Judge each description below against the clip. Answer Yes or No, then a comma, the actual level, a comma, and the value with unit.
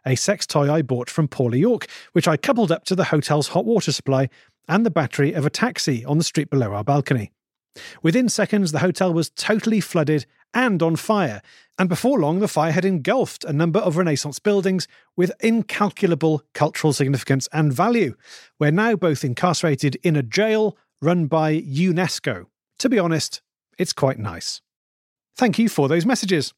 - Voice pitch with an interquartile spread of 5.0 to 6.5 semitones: Yes, average, 5.3 semitones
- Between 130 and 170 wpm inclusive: No, average, 180 wpm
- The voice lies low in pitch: No, medium, 165 Hz